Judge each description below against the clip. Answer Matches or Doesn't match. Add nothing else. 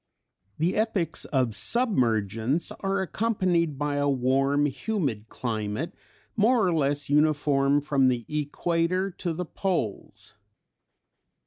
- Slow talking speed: Matches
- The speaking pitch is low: Doesn't match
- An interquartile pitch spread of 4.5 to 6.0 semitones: Matches